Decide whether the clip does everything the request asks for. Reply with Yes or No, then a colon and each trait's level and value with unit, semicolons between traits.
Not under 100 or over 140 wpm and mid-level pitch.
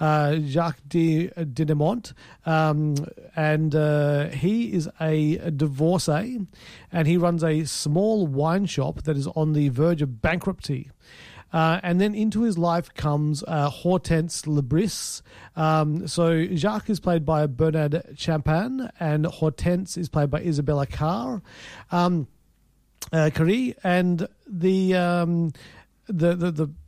Yes: slow, 135 wpm; medium, 160 Hz